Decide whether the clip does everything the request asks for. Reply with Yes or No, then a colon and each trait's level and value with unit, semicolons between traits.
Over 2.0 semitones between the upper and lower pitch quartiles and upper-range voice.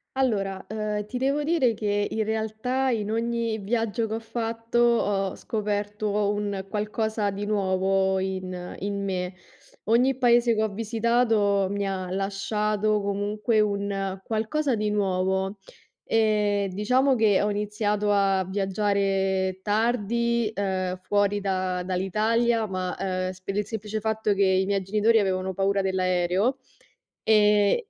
Yes: narrow, 2.4 semitones; high, 205 Hz